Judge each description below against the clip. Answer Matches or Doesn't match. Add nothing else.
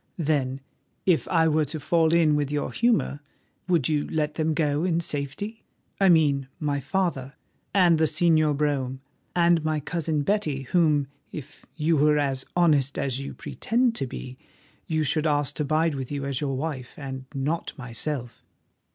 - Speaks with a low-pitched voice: Doesn't match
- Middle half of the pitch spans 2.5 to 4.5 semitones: Matches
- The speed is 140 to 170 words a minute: Matches